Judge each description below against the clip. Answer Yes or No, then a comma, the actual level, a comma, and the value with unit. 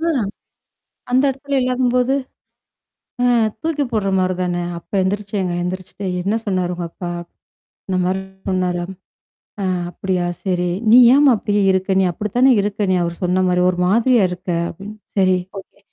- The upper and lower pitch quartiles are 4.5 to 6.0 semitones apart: No, average, 3.5 semitones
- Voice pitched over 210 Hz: No, high, 190 Hz